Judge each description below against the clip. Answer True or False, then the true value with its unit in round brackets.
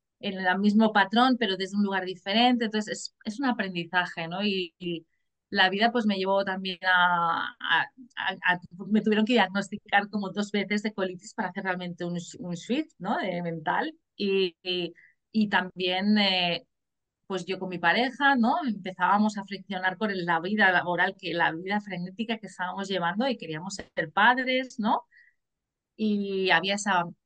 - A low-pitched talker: False (195 Hz)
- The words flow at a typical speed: True (175 wpm)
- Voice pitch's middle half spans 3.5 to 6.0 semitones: False (3.0 semitones)